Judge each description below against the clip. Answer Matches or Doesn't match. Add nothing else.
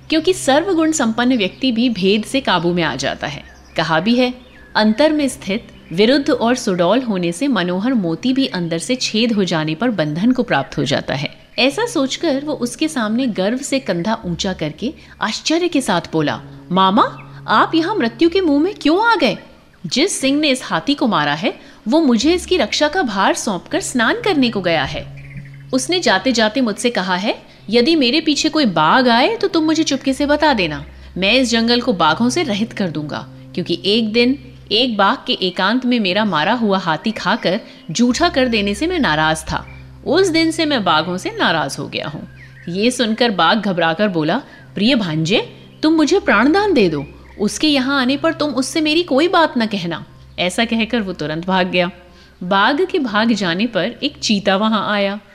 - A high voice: Matches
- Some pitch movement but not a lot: Doesn't match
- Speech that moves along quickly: Matches